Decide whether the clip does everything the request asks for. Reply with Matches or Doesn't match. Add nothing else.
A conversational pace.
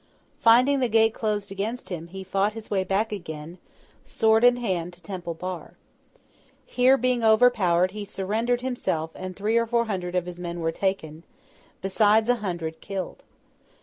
Matches